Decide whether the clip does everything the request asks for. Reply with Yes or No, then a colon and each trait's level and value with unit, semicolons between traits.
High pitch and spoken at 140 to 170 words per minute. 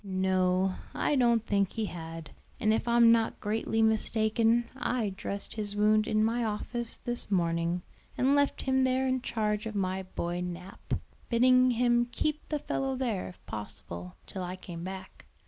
Yes: high, 215 Hz; average, 165 wpm